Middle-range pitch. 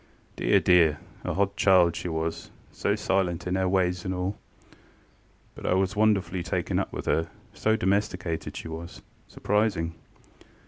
No: very low, 90 Hz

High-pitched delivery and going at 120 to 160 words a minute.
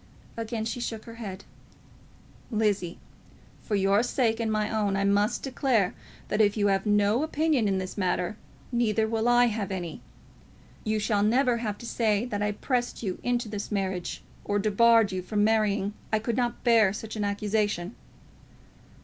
No: high, 215 Hz; average, 170 wpm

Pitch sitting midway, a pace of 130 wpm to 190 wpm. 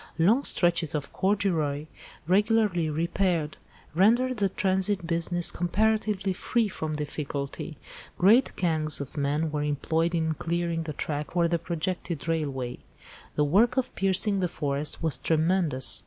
Yes: medium, 170 Hz; slow, 135 wpm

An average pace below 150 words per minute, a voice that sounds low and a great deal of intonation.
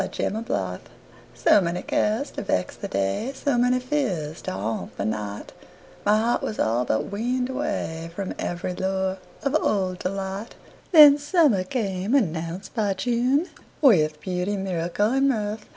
No: slow, 135 wpm; high, 195 Hz; wide, 6.4 semitones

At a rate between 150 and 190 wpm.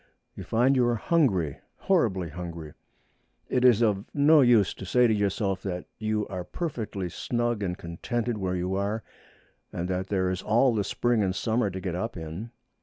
Yes: average, 180 wpm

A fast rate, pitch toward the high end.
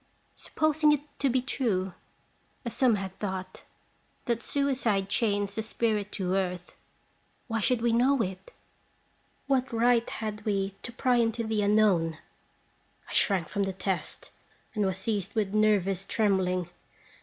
No: average, 145 wpm; high, 210 Hz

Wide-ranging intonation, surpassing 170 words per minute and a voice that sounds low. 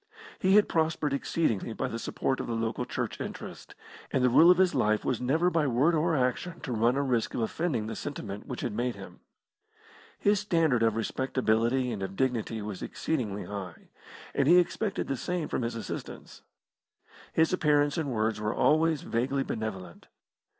Yes: wide, 6.0 semitones; average, 180 wpm; low, 125 Hz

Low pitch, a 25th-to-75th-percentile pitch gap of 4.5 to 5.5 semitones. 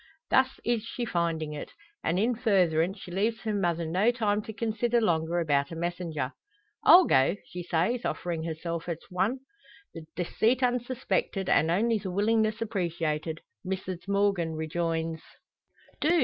No: medium, 185 Hz; average, 5.2 semitones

